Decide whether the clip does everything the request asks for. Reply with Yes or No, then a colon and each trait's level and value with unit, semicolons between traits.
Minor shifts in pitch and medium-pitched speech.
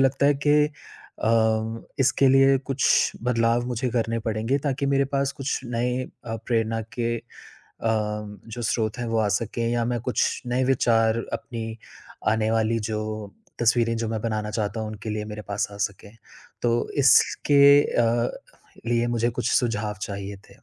No: narrow, 2.0 semitones; low, 115 Hz